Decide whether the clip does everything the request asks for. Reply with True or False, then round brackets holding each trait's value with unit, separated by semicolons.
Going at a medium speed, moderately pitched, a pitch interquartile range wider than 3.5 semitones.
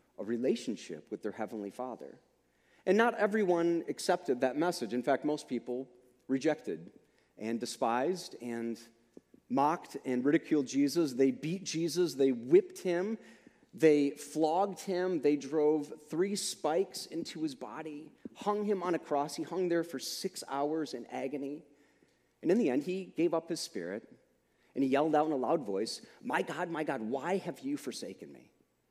True (165 wpm; 150 Hz; 5.0 semitones)